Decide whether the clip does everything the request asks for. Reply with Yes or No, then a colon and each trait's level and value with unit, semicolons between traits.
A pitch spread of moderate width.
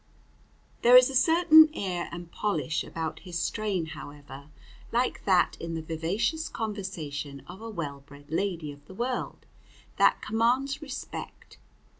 No: wide, 6.9 semitones